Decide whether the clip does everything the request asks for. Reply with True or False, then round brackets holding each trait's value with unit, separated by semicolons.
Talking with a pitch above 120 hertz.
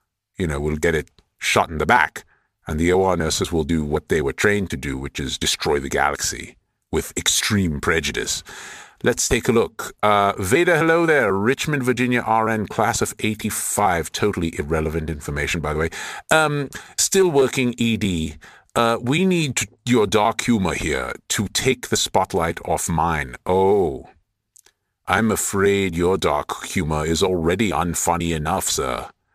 False (100 Hz)